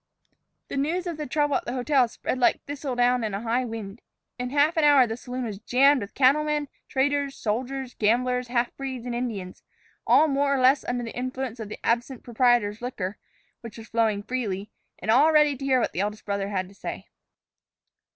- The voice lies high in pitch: Yes, very high, 250 Hz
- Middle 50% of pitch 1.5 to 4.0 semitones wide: Yes, average, 3.5 semitones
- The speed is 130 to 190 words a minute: No, average, 200 wpm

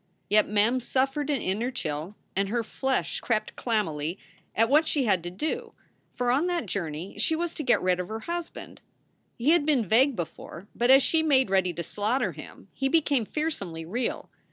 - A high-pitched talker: Yes, high, 235 Hz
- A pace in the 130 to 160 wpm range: No, average, 195 wpm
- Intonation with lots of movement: Yes, wide, 6.6 semitones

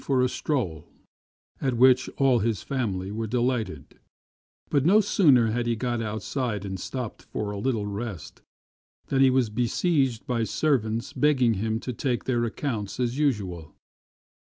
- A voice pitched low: Yes, low, 120 Hz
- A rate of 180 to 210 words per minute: No, average, 155 wpm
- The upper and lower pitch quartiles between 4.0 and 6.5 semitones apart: No, average, 3.5 semitones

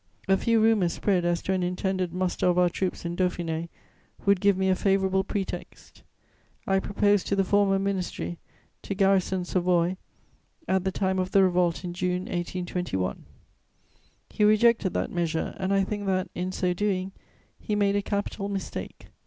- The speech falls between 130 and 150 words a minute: No, average, 170 wpm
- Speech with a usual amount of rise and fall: No, narrow, 1.8 semitones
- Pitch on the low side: No, high, 190 Hz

